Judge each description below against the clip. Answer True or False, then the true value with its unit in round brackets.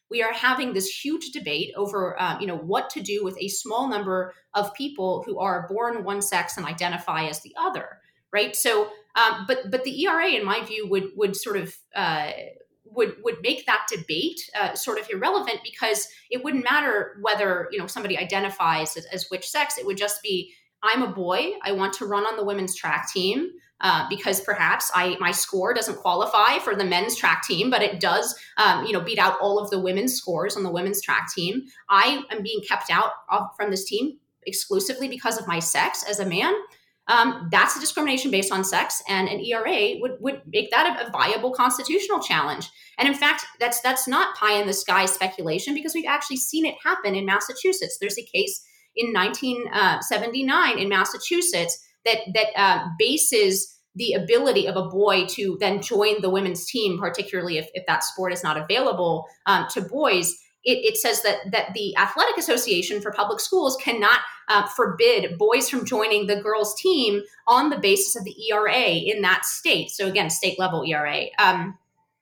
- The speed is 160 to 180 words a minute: False (195 wpm)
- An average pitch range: False (6.1 semitones)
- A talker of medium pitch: False (210 Hz)